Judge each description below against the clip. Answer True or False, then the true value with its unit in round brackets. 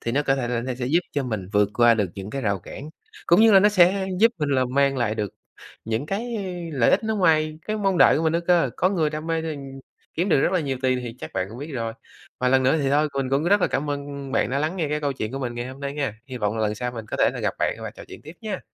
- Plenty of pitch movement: False (4.9 semitones)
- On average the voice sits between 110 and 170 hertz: True (140 Hz)